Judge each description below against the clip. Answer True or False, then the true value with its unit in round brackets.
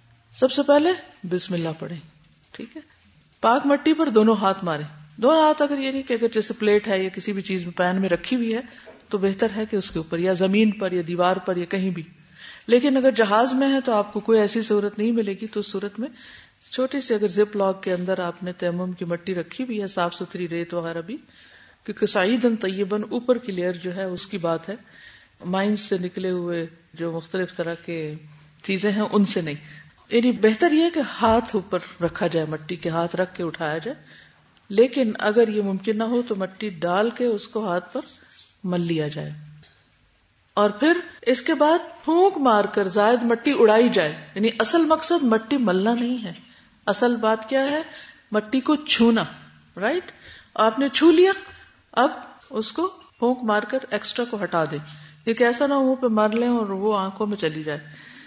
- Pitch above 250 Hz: False (210 Hz)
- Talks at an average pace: False (205 wpm)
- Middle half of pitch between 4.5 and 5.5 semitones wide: True (5.2 semitones)